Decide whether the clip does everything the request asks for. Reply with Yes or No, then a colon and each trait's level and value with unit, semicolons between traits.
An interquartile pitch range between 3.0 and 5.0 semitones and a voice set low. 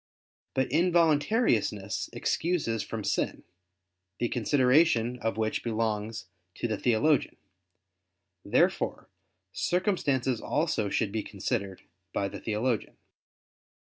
No: wide, 5.6 semitones; low, 120 Hz